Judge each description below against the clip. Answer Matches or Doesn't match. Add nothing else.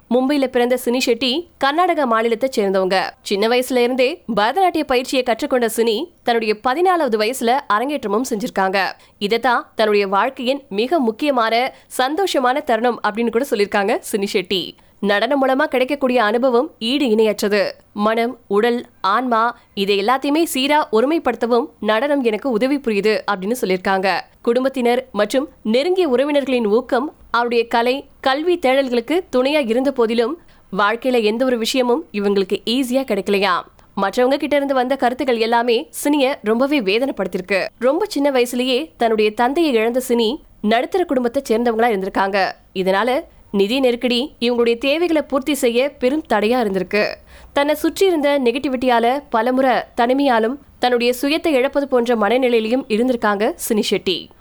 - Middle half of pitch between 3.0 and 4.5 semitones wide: Matches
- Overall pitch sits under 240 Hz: Doesn't match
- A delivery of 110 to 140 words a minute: Matches